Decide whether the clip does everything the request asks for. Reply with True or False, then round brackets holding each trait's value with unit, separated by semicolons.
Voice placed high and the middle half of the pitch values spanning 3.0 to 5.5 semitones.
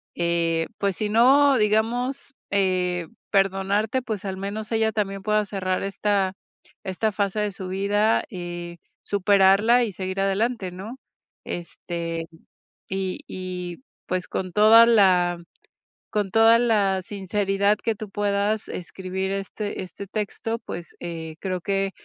False (195 Hz; 2.5 semitones)